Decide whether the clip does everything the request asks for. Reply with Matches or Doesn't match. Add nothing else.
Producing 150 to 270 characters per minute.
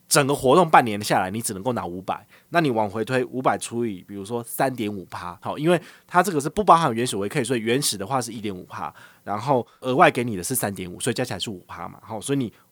Doesn't match